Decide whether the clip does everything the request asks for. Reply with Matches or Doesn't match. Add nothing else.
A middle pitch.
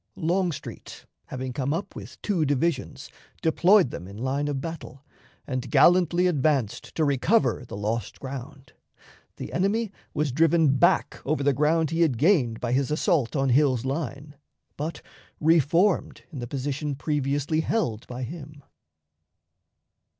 Matches